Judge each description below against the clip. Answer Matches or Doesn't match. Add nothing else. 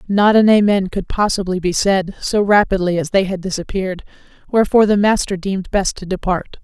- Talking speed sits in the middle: Matches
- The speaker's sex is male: Doesn't match